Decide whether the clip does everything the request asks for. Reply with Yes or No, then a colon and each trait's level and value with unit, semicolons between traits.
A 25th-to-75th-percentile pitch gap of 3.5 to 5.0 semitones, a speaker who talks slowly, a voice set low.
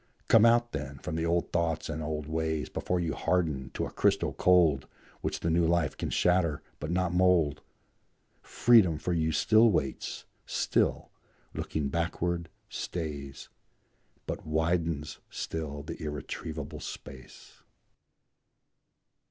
No: narrow, 2.5 semitones; slow, 125 wpm; very low, 80 Hz